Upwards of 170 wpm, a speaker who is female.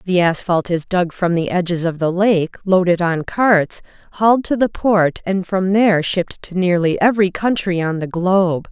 Yes: average, 195 wpm; female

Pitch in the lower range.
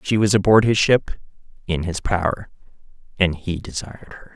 Yes: very low, 95 Hz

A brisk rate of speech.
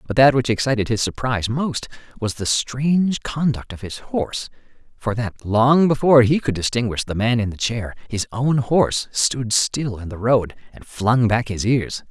No: average, 195 wpm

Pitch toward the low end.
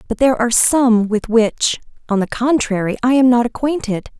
No: high, 235 Hz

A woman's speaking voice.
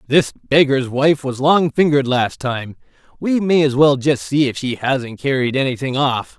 No: male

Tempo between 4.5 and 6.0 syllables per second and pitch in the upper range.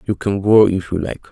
No: 5.3 syllables/s; very low, 95 Hz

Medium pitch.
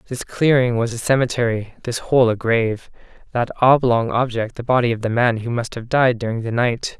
No: low, 120 Hz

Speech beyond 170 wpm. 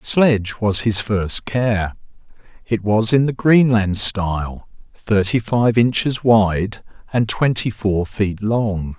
No: average, 140 wpm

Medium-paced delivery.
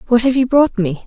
No: fast, 280 wpm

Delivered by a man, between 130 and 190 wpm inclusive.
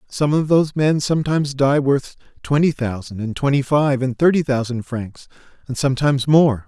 Yes: male; average, 170 wpm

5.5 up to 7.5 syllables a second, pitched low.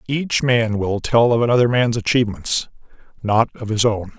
No: 4.9 syllables/s; low, 115 Hz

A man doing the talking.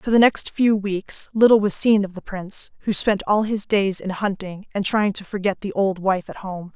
No: female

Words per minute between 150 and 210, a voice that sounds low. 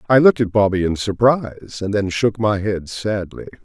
Yes: average, 200 wpm; low, 105 Hz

